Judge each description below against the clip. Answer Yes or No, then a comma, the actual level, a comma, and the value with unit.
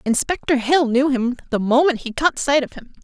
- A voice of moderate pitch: No, very high, 265 Hz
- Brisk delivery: Yes, fast, 215 wpm